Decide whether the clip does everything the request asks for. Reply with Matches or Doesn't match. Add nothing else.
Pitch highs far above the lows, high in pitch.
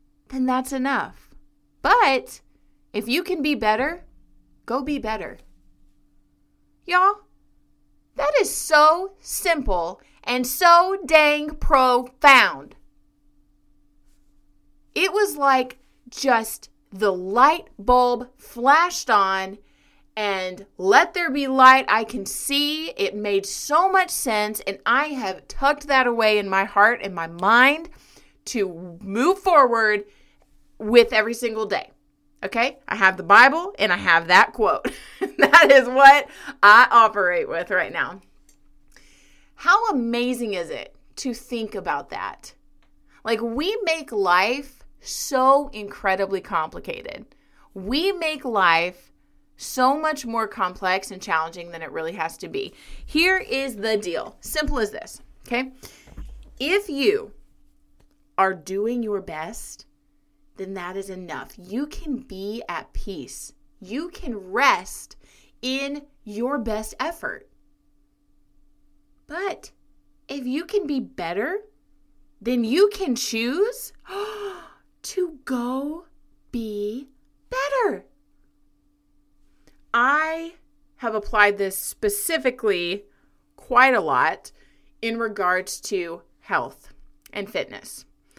Matches